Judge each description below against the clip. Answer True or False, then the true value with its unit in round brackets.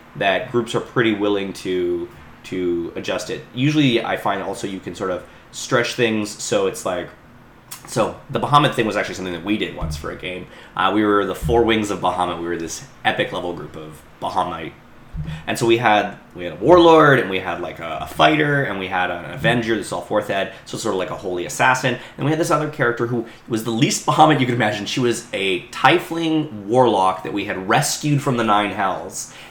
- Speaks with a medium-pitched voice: False (110 Hz)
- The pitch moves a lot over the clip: True (5.7 semitones)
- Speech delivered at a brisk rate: True (225 wpm)